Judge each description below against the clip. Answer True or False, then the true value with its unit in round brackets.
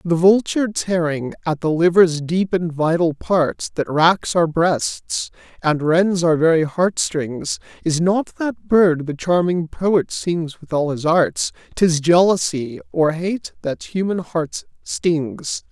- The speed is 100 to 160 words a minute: True (150 wpm)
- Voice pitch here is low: False (170 Hz)